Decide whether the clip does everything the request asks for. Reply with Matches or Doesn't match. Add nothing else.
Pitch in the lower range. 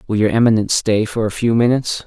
Matches